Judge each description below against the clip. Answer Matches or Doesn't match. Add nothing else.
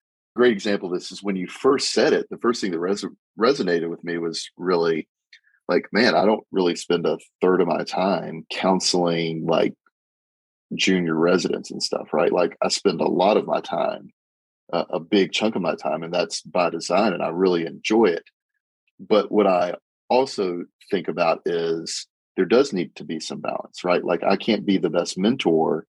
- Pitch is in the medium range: Doesn't match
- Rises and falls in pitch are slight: Doesn't match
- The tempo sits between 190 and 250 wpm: Matches